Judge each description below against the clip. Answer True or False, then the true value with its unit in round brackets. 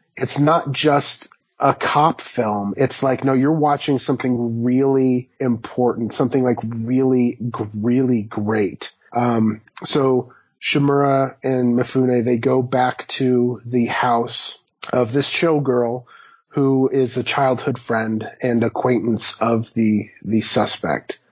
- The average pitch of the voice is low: True (125 Hz)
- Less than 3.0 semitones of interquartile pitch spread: True (2.4 semitones)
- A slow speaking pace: True (125 wpm)